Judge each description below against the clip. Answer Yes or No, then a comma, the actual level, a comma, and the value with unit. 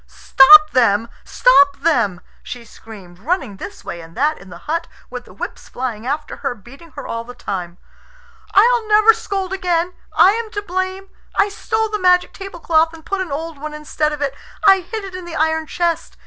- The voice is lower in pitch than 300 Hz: No, very high, 320 Hz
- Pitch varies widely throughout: Yes, wide, 7.3 semitones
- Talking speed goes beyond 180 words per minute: Yes, average, 195 wpm